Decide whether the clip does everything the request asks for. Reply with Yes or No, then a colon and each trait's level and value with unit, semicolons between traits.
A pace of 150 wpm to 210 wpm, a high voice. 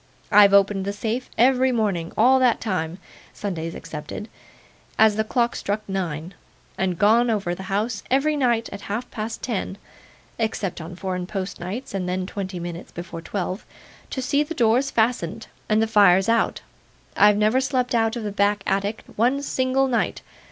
Yes: average, 170 wpm; high, 210 Hz